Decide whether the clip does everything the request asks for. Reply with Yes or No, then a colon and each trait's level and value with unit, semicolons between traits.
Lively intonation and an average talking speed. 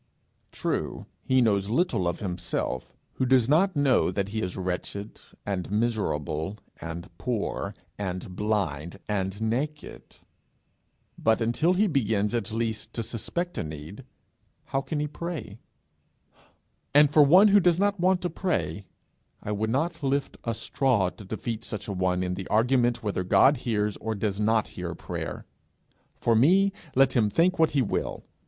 Yes: wide, 6.3 semitones; average, 160 wpm